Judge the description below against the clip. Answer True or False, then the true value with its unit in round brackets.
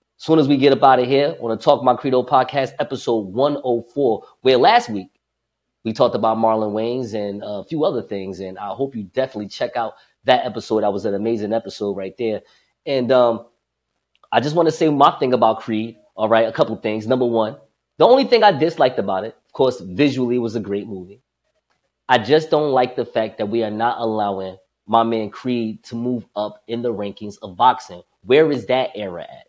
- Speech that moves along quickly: True (220 wpm)